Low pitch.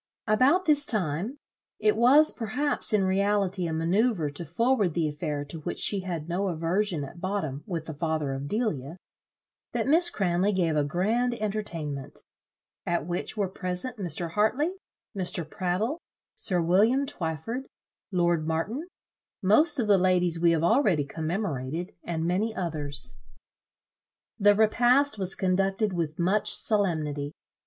No: medium, 185 Hz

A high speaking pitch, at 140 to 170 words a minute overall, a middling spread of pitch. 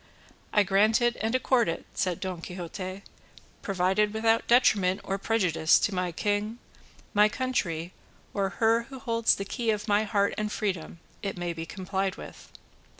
Yes: high, 200 Hz; average, 155 wpm; average, 3.4 semitones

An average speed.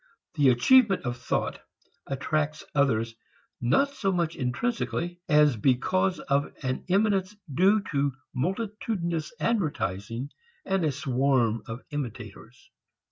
No: slow, 110 wpm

